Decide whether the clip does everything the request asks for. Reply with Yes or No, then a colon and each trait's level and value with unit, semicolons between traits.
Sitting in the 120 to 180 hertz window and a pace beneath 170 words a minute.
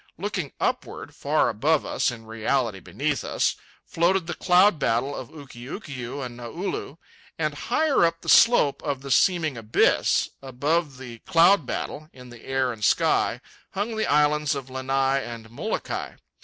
Yes: medium, 140 Hz; average, 155 wpm